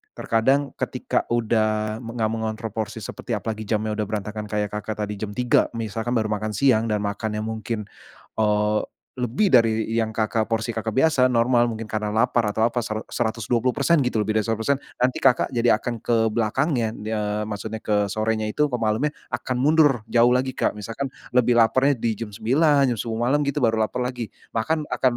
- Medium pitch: No, low, 115 Hz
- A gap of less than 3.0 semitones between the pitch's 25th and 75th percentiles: Yes, narrow, 2.4 semitones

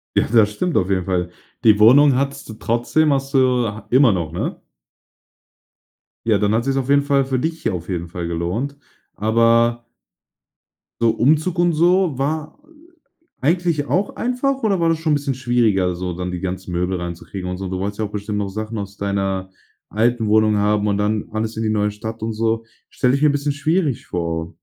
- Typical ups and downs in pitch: No, wide, 6.0 semitones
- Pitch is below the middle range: Yes, low, 115 Hz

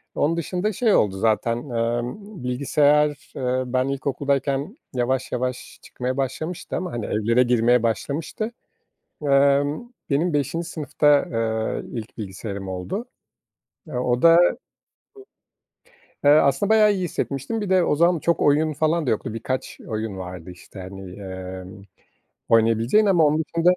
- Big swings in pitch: Yes, wide, 5.7 semitones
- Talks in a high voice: No, low, 135 Hz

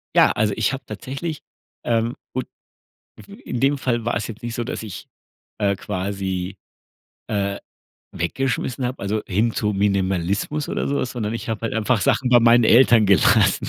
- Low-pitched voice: Yes, low, 115 Hz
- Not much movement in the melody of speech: No, average, 3.6 semitones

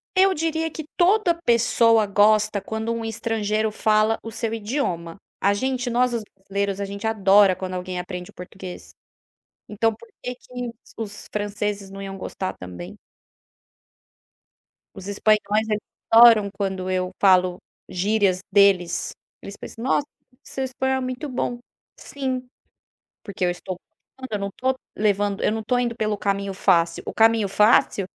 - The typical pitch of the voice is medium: No, high, 210 Hz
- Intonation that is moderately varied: Yes, average, 3.2 semitones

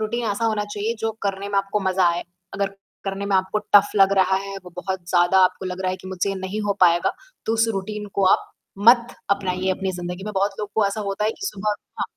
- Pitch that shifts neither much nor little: No, narrow, 1.8 semitones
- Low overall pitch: No, high, 195 Hz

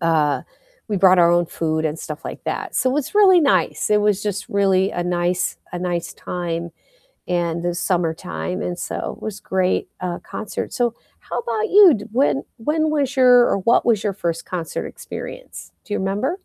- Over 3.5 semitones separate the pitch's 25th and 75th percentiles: Yes, average, 5.2 semitones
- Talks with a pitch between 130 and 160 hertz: No, high, 190 Hz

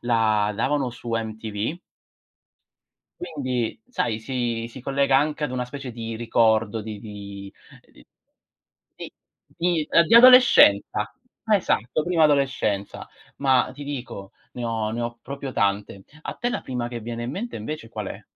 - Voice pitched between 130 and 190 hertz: No, low, 120 Hz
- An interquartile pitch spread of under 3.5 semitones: No, average, 4.2 semitones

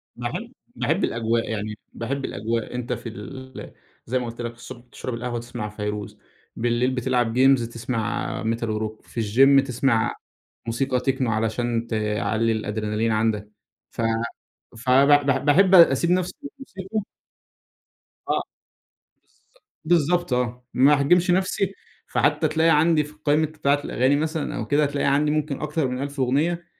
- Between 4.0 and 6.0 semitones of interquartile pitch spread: Yes, average, 4.5 semitones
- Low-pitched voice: Yes, low, 125 Hz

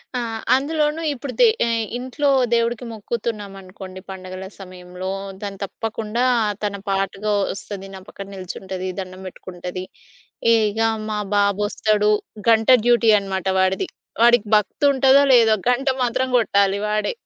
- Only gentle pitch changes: No, average, 3.6 semitones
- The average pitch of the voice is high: Yes, high, 210 Hz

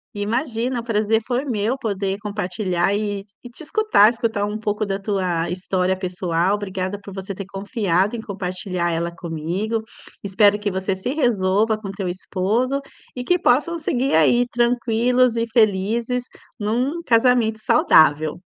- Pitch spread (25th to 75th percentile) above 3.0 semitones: Yes, average, 4.0 semitones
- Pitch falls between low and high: No, high, 210 Hz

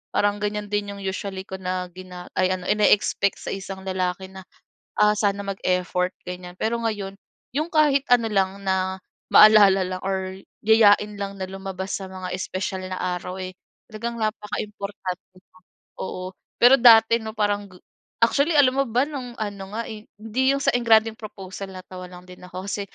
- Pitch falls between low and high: No, high, 200 Hz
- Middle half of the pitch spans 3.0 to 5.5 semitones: No, narrow, 2.4 semitones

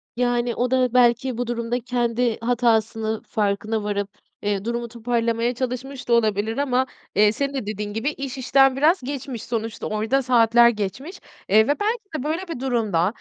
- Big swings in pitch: No, average, 2.8 semitones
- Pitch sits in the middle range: No, high, 240 Hz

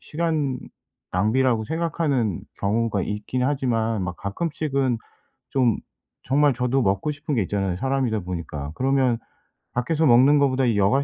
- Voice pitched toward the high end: No, low, 125 Hz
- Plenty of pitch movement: No, average, 5.0 semitones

